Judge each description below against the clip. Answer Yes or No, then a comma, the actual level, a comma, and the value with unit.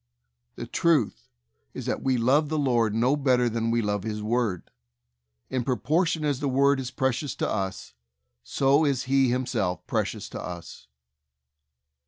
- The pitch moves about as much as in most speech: Yes, average, 3.9 semitones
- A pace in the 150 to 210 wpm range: Yes, average, 160 wpm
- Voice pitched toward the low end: Yes, low, 125 Hz